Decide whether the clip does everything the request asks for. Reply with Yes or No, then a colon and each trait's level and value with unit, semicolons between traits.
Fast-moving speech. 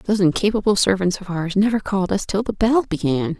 Yes: fast, 210 wpm